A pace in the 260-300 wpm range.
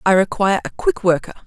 No: fast, 205 wpm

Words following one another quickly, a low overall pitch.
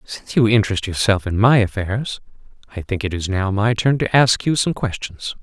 Yes: fast, 210 wpm; low, 105 Hz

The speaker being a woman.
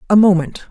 Yes: female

